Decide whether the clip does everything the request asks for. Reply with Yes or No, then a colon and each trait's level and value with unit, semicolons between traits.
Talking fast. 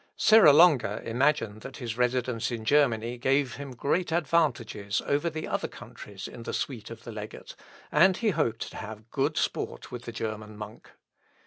No: average, 175 wpm